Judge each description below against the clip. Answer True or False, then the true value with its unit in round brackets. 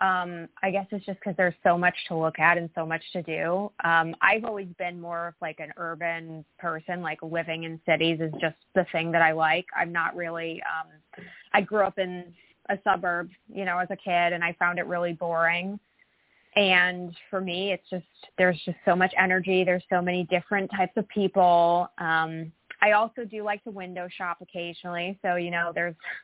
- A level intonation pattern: True (2.2 semitones)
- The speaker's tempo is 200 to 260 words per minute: True (205 wpm)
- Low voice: False (175 Hz)